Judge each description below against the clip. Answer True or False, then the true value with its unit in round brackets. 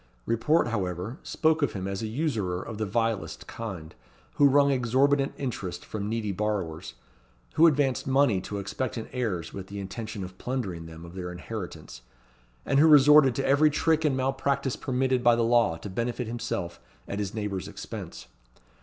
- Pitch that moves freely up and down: True (5.7 semitones)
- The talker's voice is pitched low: True (115 Hz)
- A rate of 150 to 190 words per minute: True (170 wpm)